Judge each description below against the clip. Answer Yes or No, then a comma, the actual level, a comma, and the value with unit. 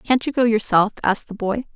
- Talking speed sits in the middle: No, fast, 240 wpm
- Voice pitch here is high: Yes, high, 225 Hz